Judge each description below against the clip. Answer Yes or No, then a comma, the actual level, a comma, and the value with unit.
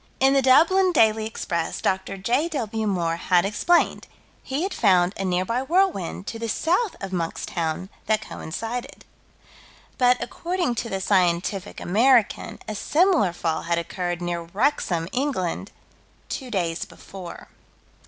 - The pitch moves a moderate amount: No, wide, 7.0 semitones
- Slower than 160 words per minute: Yes, slow, 135 wpm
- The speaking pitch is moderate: No, high, 210 Hz